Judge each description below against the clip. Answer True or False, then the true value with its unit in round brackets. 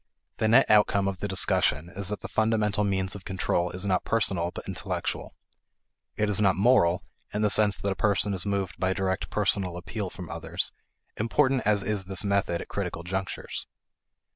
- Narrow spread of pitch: True (2.1 semitones)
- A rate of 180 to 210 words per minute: True (185 wpm)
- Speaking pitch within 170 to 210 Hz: False (100 Hz)